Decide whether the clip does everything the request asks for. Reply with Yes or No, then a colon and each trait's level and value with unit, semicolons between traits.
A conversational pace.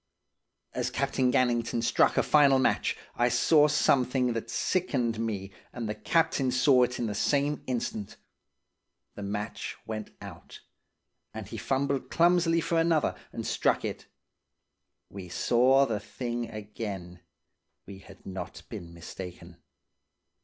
No: slow, 130 wpm